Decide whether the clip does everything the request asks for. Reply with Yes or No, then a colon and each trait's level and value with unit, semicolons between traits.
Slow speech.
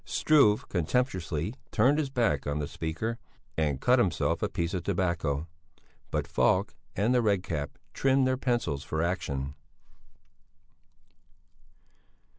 Yes: slow, 125 wpm